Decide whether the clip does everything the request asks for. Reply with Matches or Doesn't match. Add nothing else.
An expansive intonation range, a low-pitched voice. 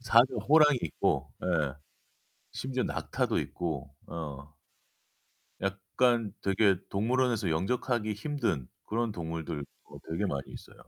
Matches